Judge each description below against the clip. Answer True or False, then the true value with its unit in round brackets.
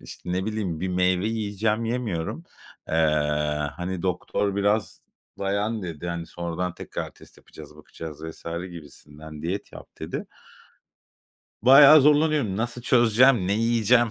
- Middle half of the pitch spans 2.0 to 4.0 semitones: False (4.6 semitones)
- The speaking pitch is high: False (100 Hz)